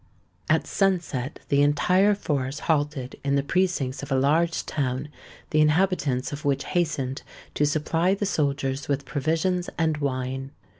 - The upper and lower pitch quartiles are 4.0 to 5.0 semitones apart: No, average, 3.6 semitones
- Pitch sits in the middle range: Yes, medium, 145 Hz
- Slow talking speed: No, average, 145 wpm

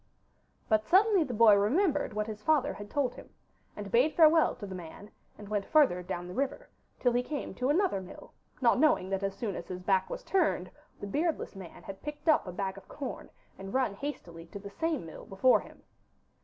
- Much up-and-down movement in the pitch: Yes, wide, 7.2 semitones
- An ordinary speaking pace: No, fast, 210 wpm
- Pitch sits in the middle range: No, high, 215 Hz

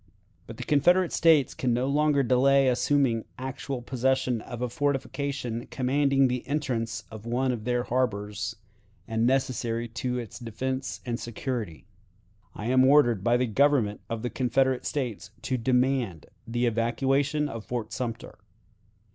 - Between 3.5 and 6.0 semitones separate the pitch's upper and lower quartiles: No, narrow, 2.6 semitones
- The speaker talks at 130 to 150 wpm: Yes, average, 145 wpm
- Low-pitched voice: Yes, low, 125 Hz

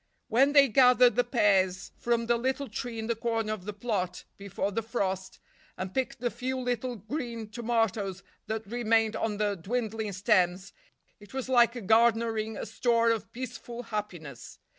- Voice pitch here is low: No, high, 225 Hz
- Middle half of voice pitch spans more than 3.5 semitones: No, average, 3.0 semitones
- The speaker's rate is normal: Yes, average, 160 wpm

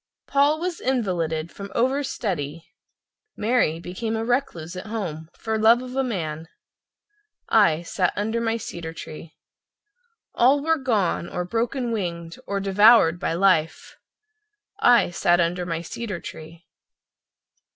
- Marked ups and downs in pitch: Yes, wide, 5.9 semitones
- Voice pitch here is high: Yes, high, 195 Hz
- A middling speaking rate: No, slow, 130 wpm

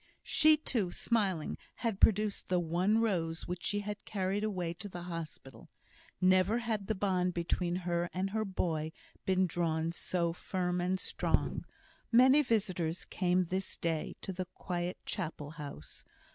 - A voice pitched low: No, medium, 185 Hz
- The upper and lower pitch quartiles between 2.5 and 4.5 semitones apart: Yes, average, 3.0 semitones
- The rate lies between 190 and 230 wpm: No, average, 150 wpm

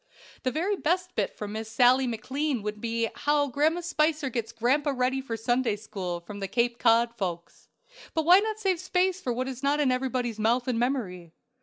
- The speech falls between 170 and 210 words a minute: Yes, average, 195 wpm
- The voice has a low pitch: No, very high, 250 Hz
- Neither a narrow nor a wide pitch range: Yes, average, 4.7 semitones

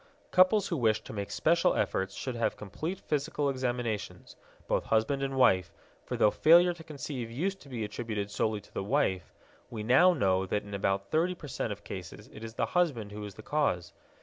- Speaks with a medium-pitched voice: No, low, 120 Hz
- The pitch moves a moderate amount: No, wide, 6.7 semitones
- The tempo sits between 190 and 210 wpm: Yes, average, 200 wpm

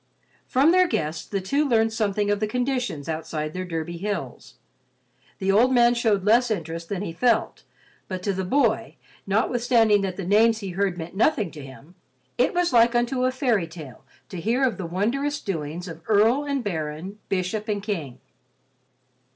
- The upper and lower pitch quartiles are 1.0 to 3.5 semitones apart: No, wide, 5.5 semitones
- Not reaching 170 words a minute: No, average, 175 wpm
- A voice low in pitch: No, high, 205 Hz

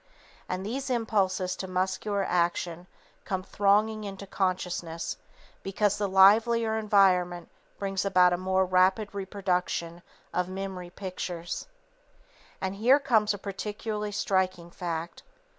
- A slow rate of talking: Yes, slow, 120 wpm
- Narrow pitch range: Yes, narrow, 2.3 semitones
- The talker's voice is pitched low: No, high, 190 Hz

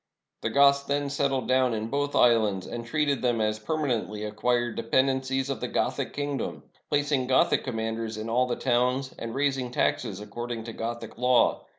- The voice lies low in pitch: Yes, low, 125 Hz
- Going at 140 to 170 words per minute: No, average, 180 wpm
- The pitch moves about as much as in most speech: Yes, average, 3.3 semitones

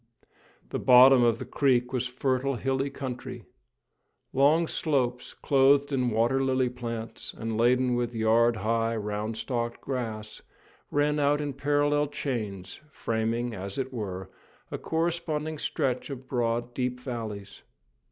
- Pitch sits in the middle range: No, low, 125 Hz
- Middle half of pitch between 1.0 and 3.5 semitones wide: Yes, average, 3.2 semitones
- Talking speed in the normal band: No, slow, 130 wpm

